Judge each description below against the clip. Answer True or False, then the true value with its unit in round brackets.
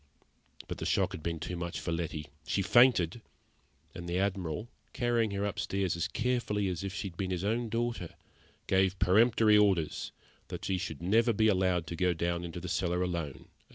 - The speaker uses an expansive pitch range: False (3.5 semitones)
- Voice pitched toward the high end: False (95 Hz)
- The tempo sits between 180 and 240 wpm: True (190 wpm)